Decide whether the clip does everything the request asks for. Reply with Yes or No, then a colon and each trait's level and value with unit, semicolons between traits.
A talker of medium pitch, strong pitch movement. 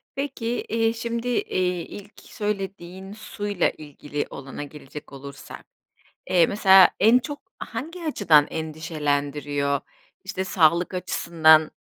Yes: medium, 180 Hz; wide, 6.2 semitones